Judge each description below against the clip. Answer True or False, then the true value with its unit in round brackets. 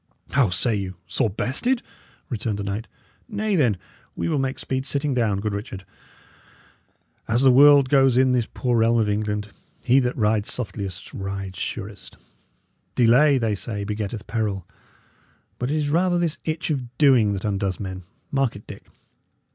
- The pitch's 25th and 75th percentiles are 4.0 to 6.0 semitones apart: True (4.8 semitones)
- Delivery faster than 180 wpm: False (165 wpm)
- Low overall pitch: True (115 Hz)